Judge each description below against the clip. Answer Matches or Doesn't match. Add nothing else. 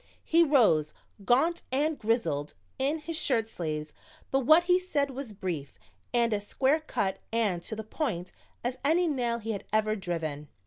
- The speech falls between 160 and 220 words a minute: Matches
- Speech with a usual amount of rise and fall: Doesn't match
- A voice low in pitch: Doesn't match